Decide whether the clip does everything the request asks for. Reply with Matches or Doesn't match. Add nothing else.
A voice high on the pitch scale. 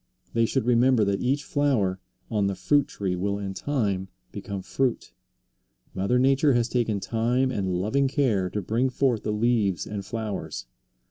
Doesn't match